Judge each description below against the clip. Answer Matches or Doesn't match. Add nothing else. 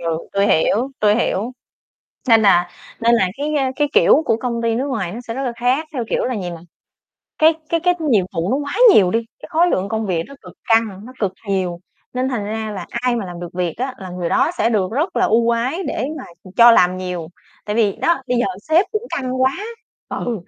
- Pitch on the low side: Doesn't match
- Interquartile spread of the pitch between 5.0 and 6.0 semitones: Matches